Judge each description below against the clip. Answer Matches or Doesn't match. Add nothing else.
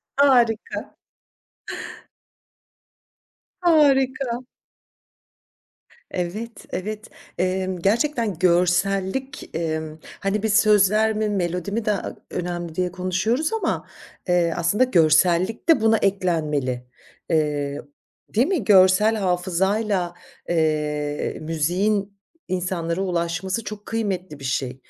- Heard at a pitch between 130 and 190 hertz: Matches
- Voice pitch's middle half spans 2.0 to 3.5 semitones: Doesn't match